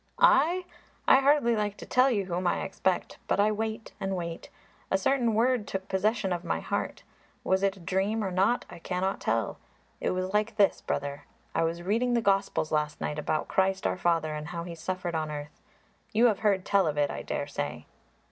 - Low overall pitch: No, high, 190 Hz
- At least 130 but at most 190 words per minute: No, fast, 205 wpm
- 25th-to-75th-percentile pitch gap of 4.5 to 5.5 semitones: No, average, 4.1 semitones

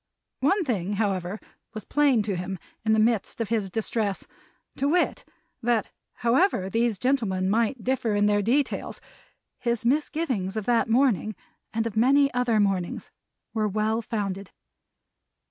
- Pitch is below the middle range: No, high, 225 Hz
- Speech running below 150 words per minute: Yes, average, 140 wpm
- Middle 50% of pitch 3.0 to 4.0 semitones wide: Yes, average, 3.3 semitones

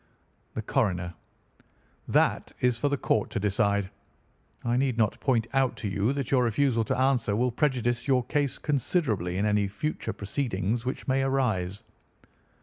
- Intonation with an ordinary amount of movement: Yes, average, 4.6 semitones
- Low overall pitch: Yes, low, 120 Hz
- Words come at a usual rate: Yes, average, 155 wpm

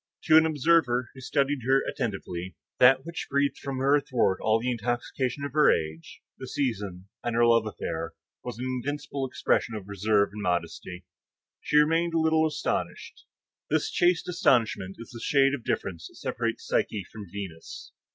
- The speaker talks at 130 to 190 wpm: Yes, average, 170 wpm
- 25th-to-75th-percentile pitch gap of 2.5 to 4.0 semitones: No, wide, 5.6 semitones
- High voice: No, low, 125 Hz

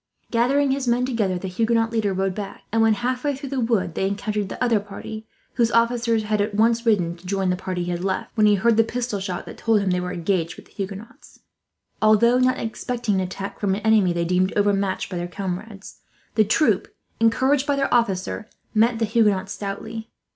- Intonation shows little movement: No, average, 3.4 semitones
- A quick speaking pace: Yes, fast, 210 wpm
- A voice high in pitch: Yes, high, 215 Hz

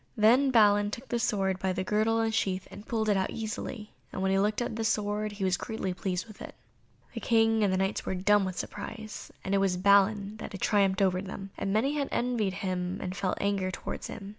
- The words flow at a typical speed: No, fast, 240 wpm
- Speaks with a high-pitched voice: Yes, high, 205 Hz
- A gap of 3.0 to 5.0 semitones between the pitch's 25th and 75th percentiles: No, narrow, 2.4 semitones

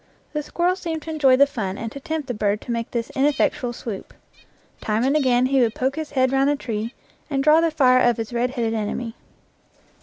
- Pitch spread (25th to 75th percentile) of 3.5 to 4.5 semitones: Yes, average, 4.0 semitones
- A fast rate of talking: Yes, fast, 220 wpm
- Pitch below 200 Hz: No, very high, 255 Hz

